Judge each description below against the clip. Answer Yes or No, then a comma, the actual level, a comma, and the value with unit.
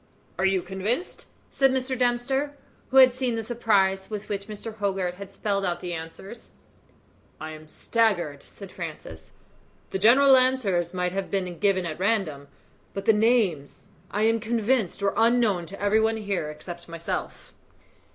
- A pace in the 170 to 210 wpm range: No, average, 160 wpm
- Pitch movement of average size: Yes, average, 4.3 semitones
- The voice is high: Yes, high, 200 Hz